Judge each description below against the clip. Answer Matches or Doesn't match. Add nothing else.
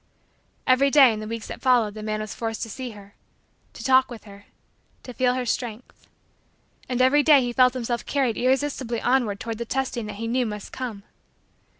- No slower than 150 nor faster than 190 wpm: Doesn't match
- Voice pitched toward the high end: Matches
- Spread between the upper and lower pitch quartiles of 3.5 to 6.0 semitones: Doesn't match